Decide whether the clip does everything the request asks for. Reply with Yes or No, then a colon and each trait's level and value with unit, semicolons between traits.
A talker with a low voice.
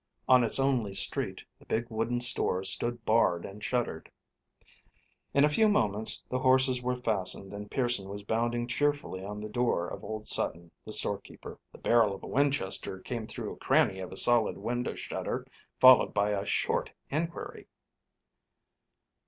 Yes: low, 115 Hz